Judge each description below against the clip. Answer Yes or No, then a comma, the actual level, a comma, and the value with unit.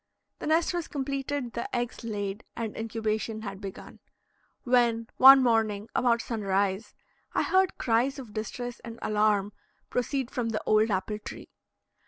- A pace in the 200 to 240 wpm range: No, average, 145 wpm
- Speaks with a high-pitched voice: Yes, high, 230 Hz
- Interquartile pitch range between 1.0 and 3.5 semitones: Yes, average, 2.8 semitones